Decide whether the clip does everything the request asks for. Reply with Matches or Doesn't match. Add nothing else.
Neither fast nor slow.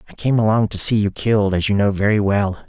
Doesn't match